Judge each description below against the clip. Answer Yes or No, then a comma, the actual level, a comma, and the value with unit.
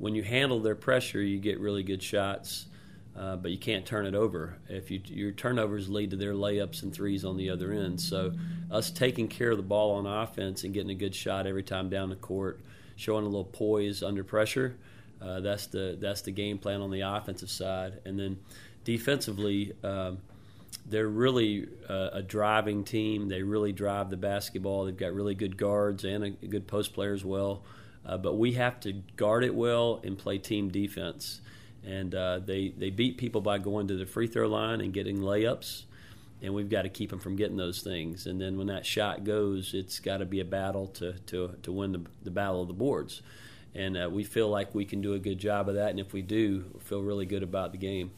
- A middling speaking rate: No, fast, 225 wpm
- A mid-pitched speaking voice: No, low, 100 Hz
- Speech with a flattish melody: Yes, narrow, 1.9 semitones